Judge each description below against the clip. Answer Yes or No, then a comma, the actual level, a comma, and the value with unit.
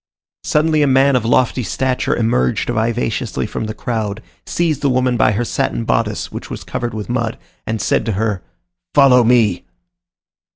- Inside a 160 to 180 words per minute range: Yes, average, 165 wpm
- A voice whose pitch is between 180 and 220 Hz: No, low, 120 Hz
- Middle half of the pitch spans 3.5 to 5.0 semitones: No, average, 2.8 semitones